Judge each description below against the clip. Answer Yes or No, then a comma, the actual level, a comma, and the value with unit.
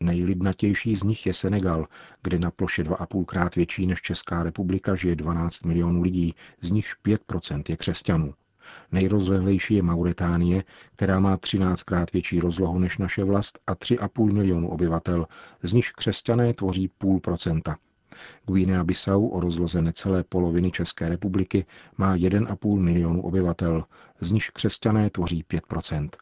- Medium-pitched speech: No, very low, 90 Hz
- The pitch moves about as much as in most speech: No, narrow, 2.2 semitones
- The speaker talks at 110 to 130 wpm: No, average, 140 wpm